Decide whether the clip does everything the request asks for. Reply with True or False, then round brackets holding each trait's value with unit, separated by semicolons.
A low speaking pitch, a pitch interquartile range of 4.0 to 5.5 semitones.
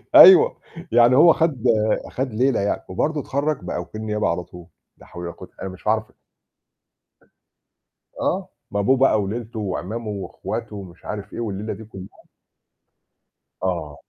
True (110 Hz; 4.8 semitones)